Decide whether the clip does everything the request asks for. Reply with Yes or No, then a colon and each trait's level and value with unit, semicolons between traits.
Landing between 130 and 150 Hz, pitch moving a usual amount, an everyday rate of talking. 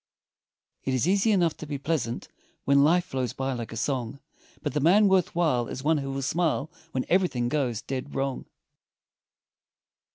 Yes: medium, 140 Hz; average, 4.3 semitones; average, 170 wpm